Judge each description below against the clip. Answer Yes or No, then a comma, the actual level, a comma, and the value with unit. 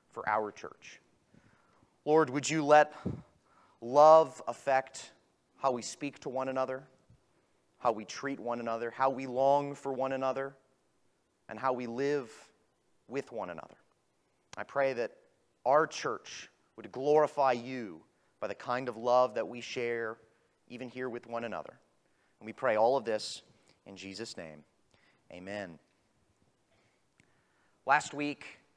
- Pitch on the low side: Yes, low, 130 Hz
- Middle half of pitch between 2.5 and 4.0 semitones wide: Yes, average, 2.9 semitones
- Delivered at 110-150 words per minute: Yes, average, 140 wpm